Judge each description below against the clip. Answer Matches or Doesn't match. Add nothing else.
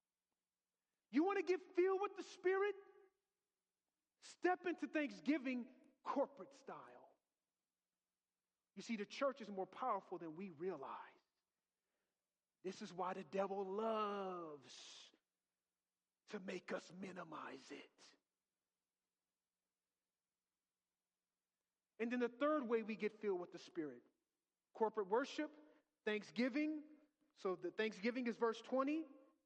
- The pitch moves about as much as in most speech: Doesn't match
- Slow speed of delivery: Matches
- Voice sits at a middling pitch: Doesn't match